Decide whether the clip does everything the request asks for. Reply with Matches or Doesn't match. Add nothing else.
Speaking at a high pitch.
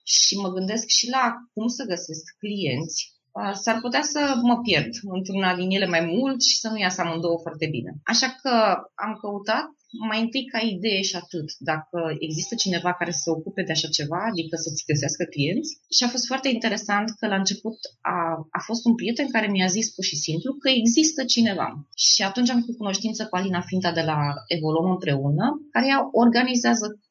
Matches